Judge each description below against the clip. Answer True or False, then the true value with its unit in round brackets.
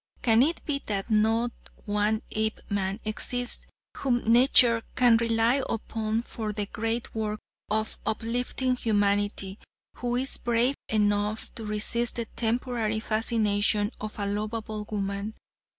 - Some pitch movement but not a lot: False (2.0 semitones)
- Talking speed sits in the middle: False (125 wpm)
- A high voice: True (220 Hz)